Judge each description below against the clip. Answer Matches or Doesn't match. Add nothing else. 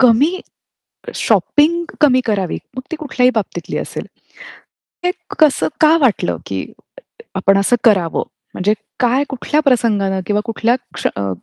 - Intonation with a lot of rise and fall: Matches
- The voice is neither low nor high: Doesn't match